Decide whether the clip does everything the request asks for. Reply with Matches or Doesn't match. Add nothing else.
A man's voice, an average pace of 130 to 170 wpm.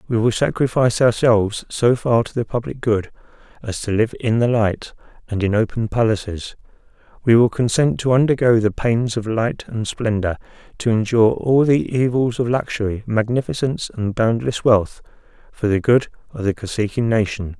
Matches